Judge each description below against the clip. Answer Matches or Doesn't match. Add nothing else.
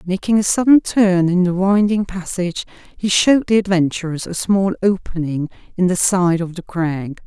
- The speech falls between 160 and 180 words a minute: Matches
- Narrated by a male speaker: Doesn't match